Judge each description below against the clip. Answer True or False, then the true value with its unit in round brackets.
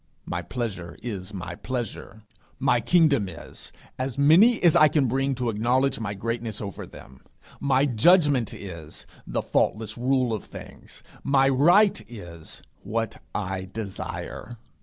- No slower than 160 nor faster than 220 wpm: False (140 wpm)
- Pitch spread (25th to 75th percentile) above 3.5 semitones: True (5.1 semitones)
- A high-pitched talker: False (120 Hz)